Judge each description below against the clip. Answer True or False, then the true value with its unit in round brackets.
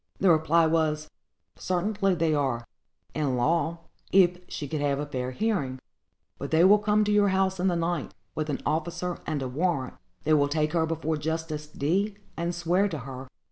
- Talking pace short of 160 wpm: False (185 wpm)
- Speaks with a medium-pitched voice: True (160 Hz)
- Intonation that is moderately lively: True (3.5 semitones)